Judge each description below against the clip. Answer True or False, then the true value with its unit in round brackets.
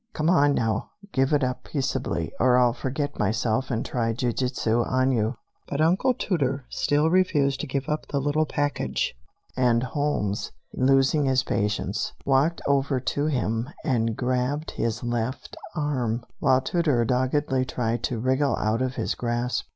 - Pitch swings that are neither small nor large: True (3.3 semitones)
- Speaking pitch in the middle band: False (130 Hz)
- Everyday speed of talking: True (160 wpm)